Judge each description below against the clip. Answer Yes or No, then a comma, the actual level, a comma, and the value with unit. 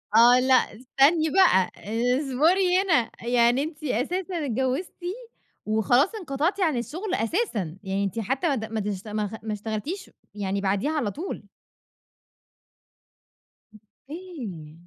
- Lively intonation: Yes, wide, 7.0 semitones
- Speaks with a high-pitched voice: Yes, very high, 255 Hz